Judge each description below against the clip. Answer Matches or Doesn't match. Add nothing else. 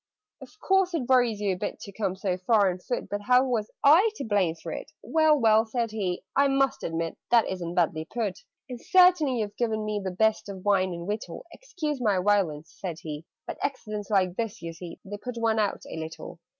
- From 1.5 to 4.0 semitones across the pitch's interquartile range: Doesn't match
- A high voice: Matches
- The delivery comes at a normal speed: Doesn't match